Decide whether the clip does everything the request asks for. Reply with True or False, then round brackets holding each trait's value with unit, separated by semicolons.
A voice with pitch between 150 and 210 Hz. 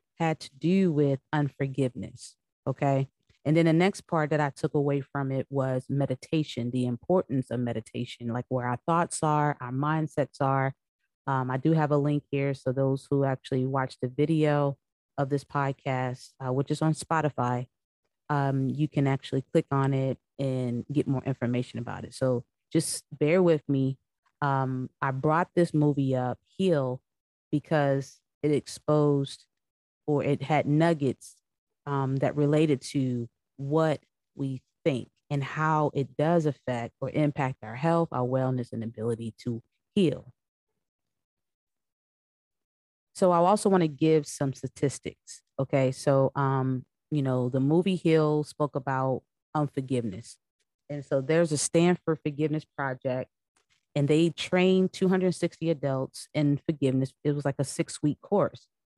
False (140 Hz)